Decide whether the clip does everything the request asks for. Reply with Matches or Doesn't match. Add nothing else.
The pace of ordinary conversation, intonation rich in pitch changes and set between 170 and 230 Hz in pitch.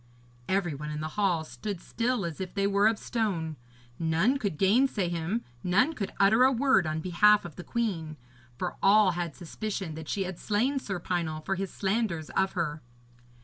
Doesn't match